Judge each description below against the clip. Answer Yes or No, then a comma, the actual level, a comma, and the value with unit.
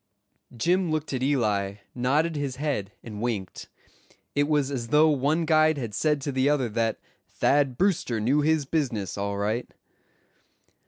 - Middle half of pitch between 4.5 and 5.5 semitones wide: Yes, average, 4.8 semitones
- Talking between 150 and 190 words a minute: Yes, average, 155 wpm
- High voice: No, low, 135 Hz